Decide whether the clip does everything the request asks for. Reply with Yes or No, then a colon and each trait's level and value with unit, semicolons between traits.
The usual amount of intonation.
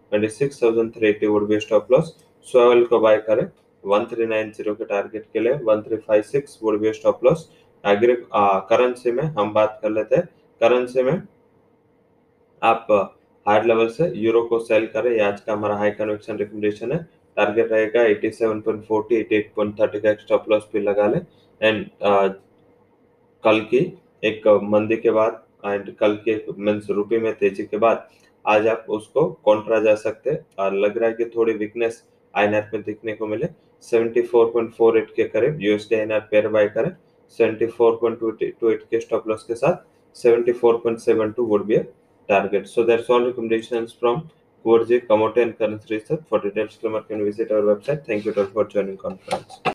No: narrow, 1.8 semitones